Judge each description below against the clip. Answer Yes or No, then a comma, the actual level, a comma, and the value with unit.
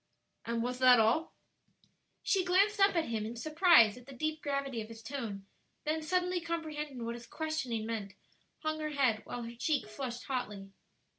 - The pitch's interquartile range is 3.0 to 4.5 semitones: No, average, 5.3 semitones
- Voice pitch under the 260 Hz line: No, very high, 265 Hz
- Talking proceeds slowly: No, average, 175 wpm